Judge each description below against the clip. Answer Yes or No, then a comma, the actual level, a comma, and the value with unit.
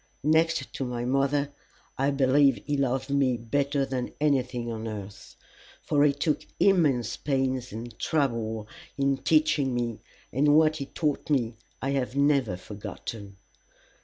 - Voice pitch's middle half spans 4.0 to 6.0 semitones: No, average, 3.1 semitones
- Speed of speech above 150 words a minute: No, average, 140 wpm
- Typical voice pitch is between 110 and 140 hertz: Yes, low, 135 Hz